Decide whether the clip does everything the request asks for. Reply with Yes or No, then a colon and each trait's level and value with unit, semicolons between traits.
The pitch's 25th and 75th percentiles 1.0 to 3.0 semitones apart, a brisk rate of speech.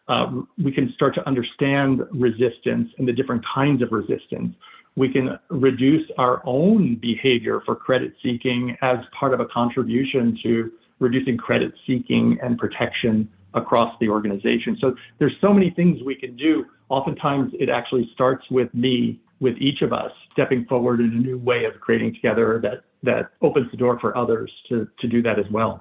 No: narrow, 2.4 semitones; average, 175 wpm